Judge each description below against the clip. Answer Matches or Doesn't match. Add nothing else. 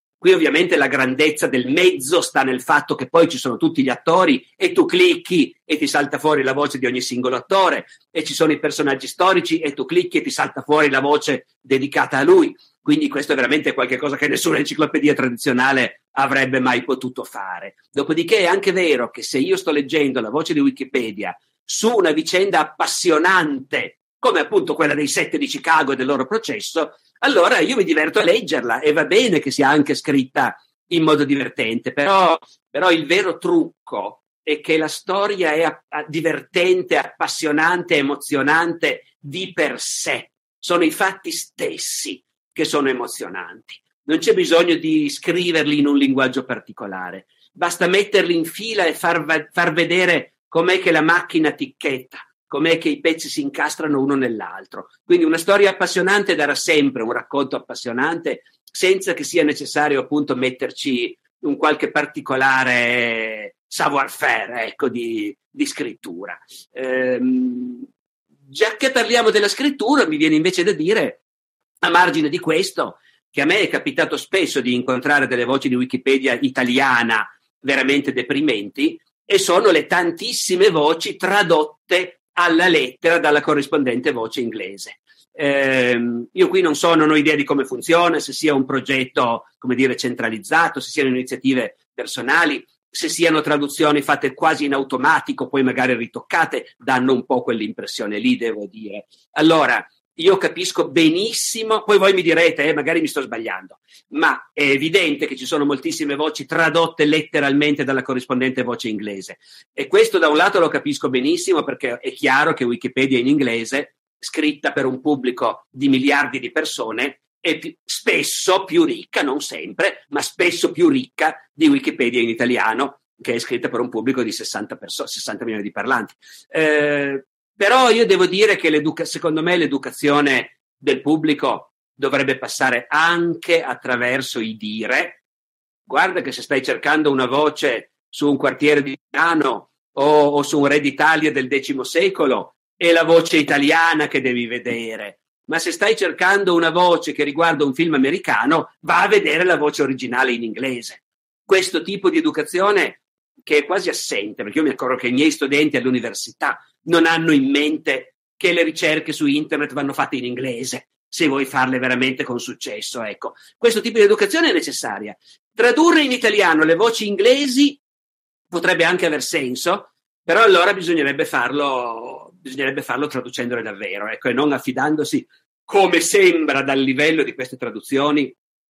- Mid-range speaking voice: Matches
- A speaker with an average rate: Matches